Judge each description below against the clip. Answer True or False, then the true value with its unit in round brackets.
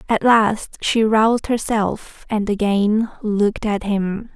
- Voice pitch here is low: False (215 Hz)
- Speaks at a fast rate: False (140 wpm)